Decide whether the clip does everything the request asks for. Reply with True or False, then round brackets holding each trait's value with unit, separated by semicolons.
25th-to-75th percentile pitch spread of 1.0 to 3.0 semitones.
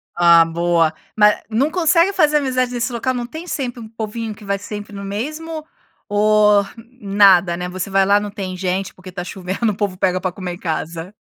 False (4.6 semitones)